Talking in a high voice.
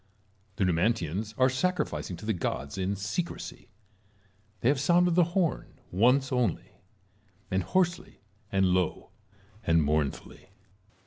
No: low, 105 Hz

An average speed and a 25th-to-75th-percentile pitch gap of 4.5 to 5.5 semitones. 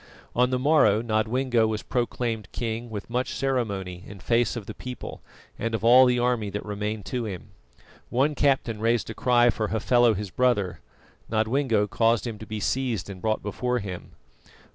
No: average, 175 wpm; average, 2.9 semitones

